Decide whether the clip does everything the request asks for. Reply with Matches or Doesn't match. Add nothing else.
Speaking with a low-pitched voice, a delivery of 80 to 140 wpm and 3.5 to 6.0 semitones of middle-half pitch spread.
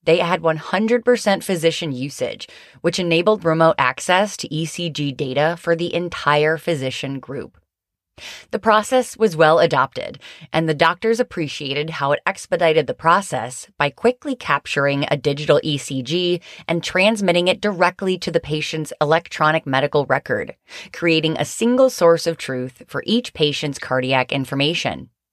Doesn't match